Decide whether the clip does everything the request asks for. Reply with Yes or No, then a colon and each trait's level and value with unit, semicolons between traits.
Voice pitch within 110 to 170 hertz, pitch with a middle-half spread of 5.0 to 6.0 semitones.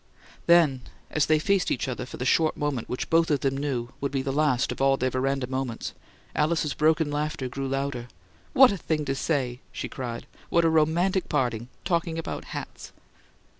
No: medium, 140 Hz; average, 3.5 semitones